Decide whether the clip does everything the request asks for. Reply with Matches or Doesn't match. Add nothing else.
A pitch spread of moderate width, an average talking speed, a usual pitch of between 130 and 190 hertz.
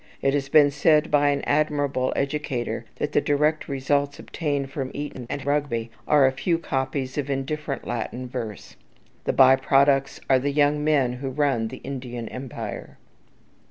Doesn't match